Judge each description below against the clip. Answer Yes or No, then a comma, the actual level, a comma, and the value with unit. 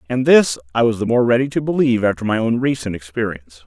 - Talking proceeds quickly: Yes, fast, 230 wpm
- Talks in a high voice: No, low, 115 Hz